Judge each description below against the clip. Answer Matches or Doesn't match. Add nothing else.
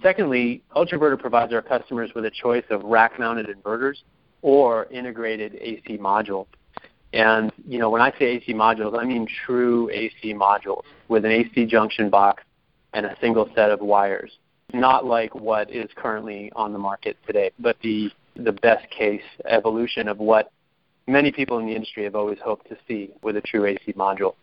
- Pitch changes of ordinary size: Doesn't match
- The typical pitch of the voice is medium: Doesn't match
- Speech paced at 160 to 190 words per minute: Matches